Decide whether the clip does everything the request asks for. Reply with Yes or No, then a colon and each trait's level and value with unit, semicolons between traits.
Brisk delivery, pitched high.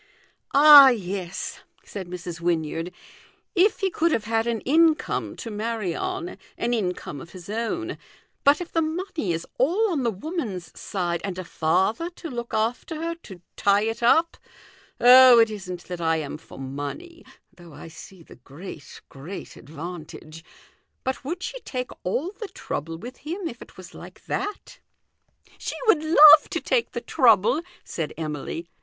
No: average, 170 wpm; high, 225 Hz